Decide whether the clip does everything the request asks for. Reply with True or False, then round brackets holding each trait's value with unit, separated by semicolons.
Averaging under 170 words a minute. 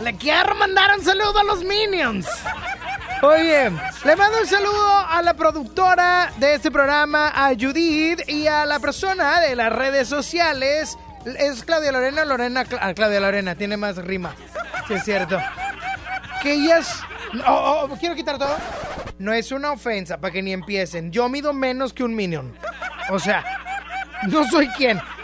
True (160 wpm)